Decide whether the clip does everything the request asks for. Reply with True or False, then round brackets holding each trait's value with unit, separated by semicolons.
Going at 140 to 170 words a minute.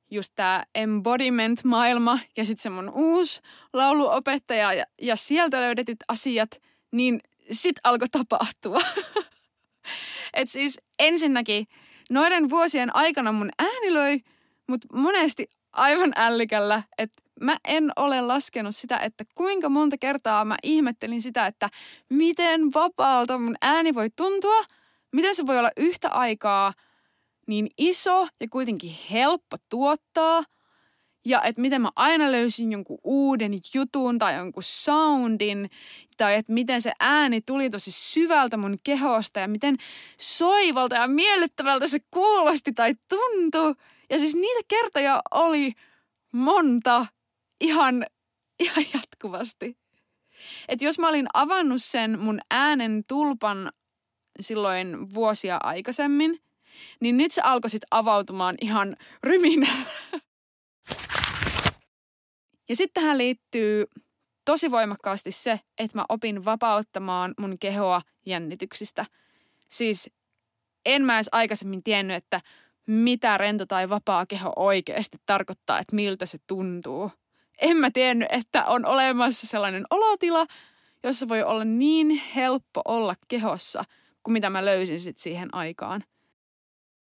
False (120 wpm)